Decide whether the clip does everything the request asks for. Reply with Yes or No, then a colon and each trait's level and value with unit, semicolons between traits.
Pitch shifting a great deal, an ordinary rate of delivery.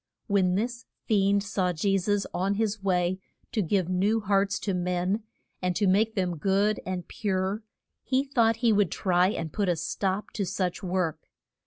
No: narrow, 2.4 semitones; average, 175 wpm